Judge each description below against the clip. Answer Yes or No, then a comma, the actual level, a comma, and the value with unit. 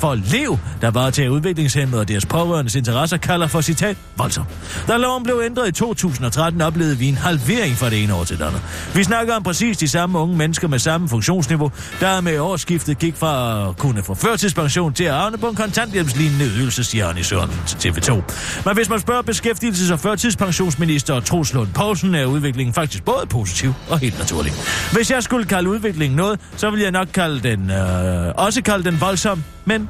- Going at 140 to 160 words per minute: No, average, 195 wpm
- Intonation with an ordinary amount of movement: No, wide, 7.6 semitones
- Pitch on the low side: No, medium, 165 Hz